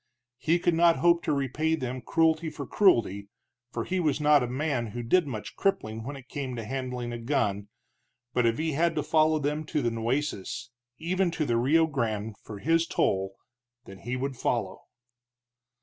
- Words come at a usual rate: Yes, average, 185 wpm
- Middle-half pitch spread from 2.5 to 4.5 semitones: No, average, 5.3 semitones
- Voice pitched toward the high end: No, low, 135 Hz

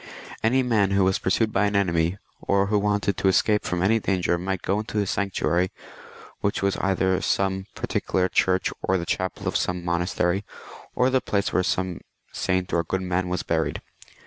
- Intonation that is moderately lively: No, narrow, 1.9 semitones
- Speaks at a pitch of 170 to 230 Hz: No, very low, 95 Hz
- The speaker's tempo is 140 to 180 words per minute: No, average, 190 wpm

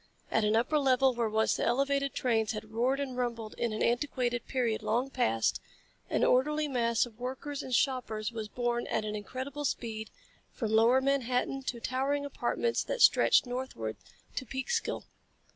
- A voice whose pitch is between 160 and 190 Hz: No, high, 245 Hz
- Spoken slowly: No, average, 165 wpm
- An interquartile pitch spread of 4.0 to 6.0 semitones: No, average, 3.2 semitones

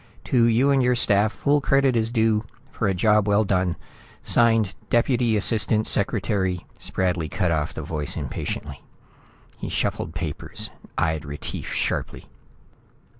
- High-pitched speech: No, low, 105 Hz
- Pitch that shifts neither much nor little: Yes, average, 4.5 semitones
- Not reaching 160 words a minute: Yes, average, 140 wpm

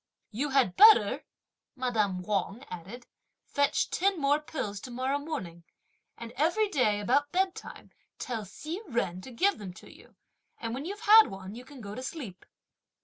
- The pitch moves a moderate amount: No, wide, 6.9 semitones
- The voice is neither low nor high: No, very high, 255 Hz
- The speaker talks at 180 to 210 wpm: No, average, 160 wpm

